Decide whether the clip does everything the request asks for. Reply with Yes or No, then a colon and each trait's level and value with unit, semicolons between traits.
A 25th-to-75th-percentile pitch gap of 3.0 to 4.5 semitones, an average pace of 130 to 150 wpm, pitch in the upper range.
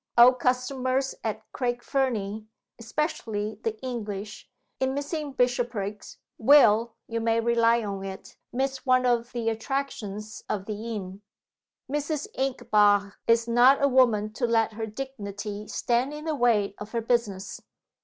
Yes: average, 3.5 semitones; average, 140 wpm; high, 235 Hz